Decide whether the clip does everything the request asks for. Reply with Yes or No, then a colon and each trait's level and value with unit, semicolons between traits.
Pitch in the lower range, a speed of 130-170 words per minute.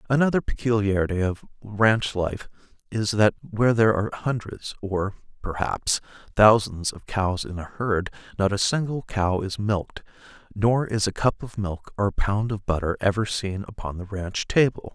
Yes: low, 105 Hz; average, 165 wpm